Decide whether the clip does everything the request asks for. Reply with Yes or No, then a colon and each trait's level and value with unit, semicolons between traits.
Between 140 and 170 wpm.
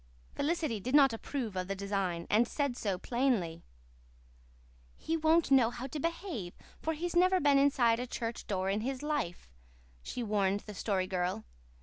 Yes: average, 165 wpm